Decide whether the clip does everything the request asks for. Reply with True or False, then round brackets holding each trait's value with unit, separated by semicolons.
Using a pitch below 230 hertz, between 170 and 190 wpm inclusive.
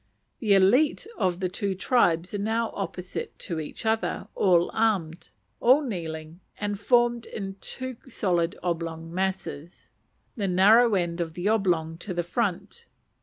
False (190 Hz; 145 wpm)